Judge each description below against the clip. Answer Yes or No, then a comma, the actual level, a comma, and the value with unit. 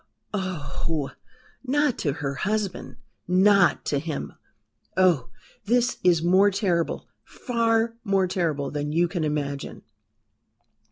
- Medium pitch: Yes, medium, 180 Hz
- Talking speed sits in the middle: No, slow, 110 wpm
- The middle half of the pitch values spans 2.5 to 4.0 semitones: No, average, 5.3 semitones